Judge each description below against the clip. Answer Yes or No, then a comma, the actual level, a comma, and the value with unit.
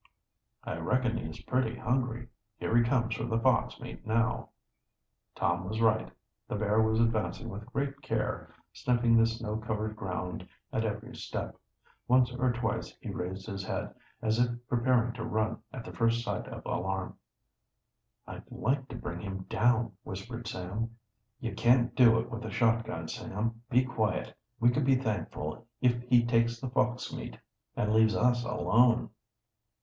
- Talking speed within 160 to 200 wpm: Yes, average, 165 wpm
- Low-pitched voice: Yes, low, 115 Hz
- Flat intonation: Yes, narrow, 2.1 semitones